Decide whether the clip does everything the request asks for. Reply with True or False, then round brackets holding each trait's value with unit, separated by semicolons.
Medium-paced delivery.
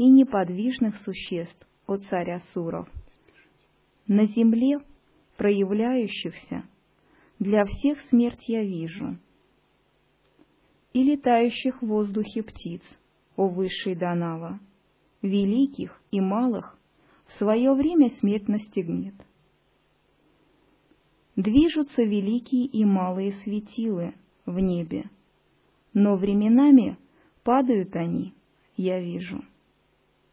False (85 wpm)